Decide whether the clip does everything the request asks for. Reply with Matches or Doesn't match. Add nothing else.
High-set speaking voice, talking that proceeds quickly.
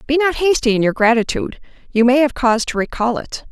Matches